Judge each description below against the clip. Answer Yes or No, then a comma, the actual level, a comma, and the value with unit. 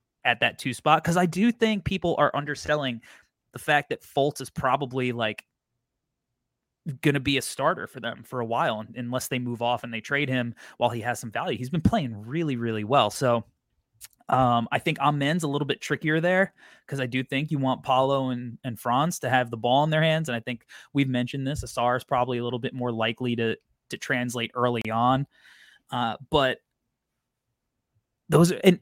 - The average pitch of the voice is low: Yes, low, 130 Hz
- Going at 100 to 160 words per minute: No, average, 200 wpm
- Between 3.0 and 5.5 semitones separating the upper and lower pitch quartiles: Yes, average, 3.3 semitones